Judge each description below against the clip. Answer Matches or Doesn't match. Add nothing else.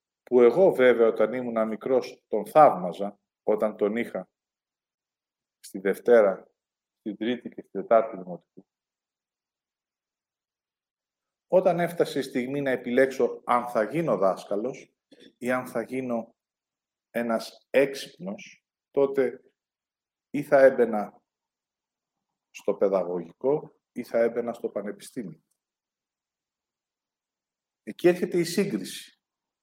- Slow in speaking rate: Matches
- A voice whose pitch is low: Matches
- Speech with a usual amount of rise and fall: Matches